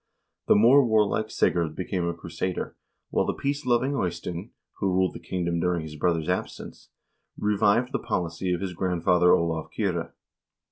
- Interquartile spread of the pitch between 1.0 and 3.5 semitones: No, average, 4.0 semitones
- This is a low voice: Yes, very low, 90 Hz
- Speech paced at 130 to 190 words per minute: Yes, average, 155 wpm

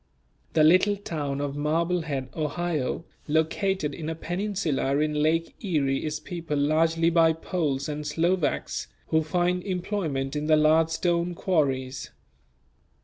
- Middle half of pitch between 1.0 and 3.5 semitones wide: Yes, average, 2.7 semitones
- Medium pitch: Yes, medium, 160 Hz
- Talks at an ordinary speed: No, slow, 130 wpm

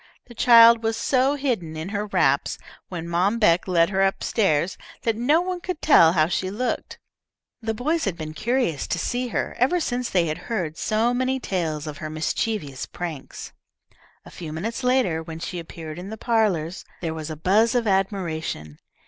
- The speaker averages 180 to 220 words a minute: Yes, average, 185 wpm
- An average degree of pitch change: No, wide, 6.4 semitones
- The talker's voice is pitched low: No, high, 195 Hz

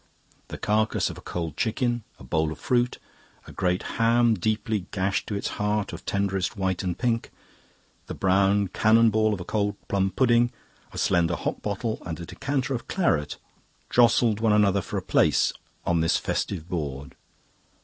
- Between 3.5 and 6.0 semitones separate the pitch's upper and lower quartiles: Yes, average, 4.1 semitones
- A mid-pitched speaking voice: No, low, 100 Hz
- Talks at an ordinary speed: Yes, average, 170 wpm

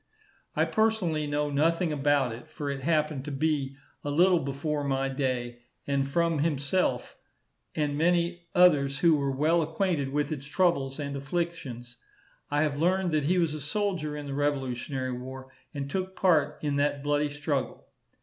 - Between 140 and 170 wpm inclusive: Yes, average, 165 wpm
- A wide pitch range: No, average, 3.2 semitones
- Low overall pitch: No, medium, 145 Hz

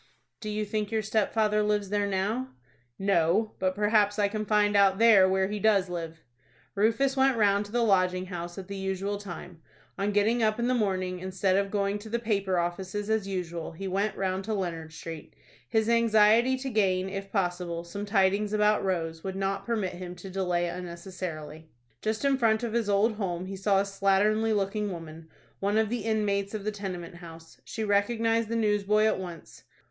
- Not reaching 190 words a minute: No, average, 195 wpm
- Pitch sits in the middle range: No, high, 200 Hz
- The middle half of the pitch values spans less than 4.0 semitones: Yes, narrow, 2.5 semitones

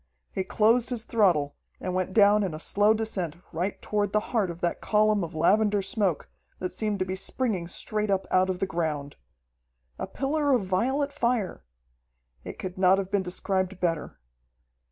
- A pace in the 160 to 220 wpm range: Yes, average, 175 wpm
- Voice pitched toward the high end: Yes, high, 195 Hz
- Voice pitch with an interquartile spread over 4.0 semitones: No, average, 2.9 semitones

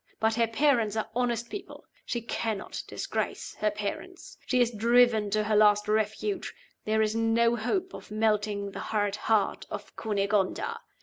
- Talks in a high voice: Yes, high, 220 Hz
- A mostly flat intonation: Yes, narrow, 2.0 semitones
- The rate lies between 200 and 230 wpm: No, average, 160 wpm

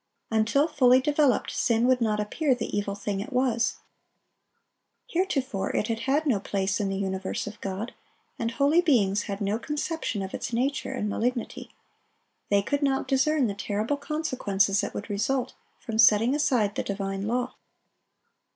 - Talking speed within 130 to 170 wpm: Yes, average, 160 wpm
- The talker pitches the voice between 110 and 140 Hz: No, high, 230 Hz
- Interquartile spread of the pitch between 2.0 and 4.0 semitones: No, average, 5.0 semitones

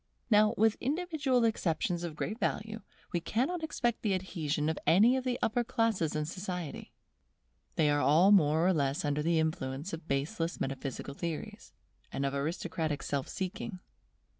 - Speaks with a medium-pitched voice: Yes, medium, 175 Hz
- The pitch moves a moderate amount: No, wide, 6.7 semitones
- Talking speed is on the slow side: No, average, 160 wpm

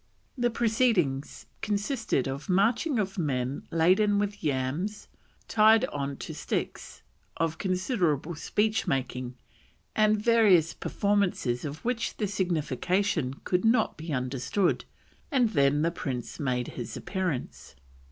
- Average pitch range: No, wide, 7.3 semitones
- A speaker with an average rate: No, slow, 120 wpm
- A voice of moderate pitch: Yes, medium, 180 Hz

